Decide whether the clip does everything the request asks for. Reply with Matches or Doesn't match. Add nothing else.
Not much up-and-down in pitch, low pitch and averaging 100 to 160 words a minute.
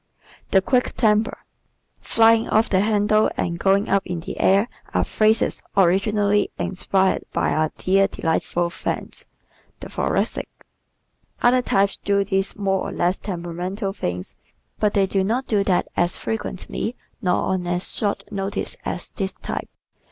Doesn't match